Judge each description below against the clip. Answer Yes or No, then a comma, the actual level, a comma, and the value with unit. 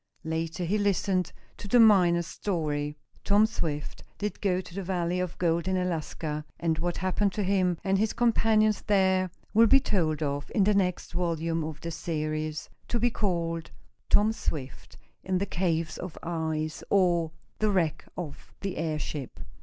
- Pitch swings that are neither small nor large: Yes, average, 3.6 semitones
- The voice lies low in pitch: No, medium, 175 Hz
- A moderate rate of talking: Yes, average, 165 wpm